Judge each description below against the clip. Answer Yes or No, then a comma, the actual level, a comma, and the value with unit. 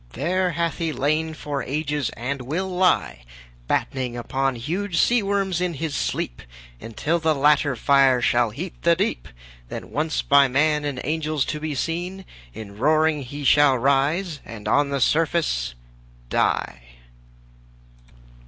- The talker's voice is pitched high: No, medium, 150 Hz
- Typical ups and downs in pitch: Yes, average, 3.7 semitones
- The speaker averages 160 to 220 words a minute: No, average, 140 wpm